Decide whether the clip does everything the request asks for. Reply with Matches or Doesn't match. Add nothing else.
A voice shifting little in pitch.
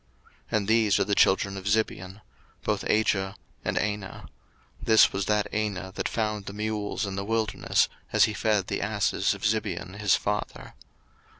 Matches